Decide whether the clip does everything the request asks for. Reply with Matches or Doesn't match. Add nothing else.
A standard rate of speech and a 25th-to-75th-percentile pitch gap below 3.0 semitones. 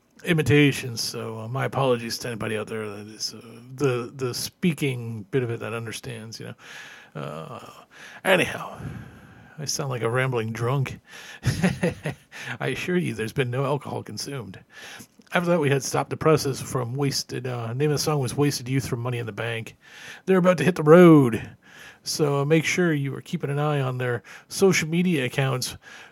Doesn't match